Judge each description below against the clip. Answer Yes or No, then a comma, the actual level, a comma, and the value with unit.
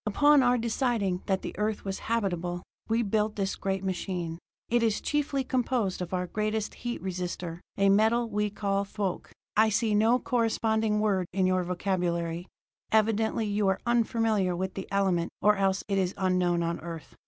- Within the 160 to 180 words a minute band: Yes, average, 170 wpm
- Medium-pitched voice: No, high, 200 Hz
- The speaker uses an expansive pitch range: No, average, 3.3 semitones